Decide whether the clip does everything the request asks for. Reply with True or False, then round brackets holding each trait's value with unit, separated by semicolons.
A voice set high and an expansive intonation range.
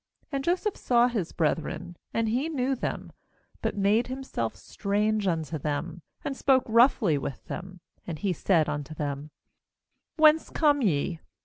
True (200 Hz; 8.4 semitones)